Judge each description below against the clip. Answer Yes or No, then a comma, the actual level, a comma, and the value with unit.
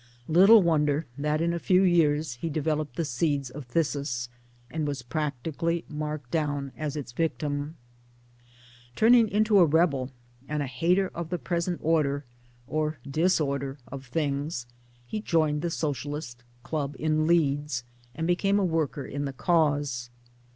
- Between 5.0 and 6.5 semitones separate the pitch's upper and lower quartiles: No, average, 3.0 semitones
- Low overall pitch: No, medium, 150 Hz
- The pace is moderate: Yes, average, 145 wpm